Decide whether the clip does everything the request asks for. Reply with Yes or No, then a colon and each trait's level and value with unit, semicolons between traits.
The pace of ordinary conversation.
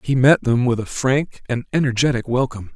Yes: average, 195 wpm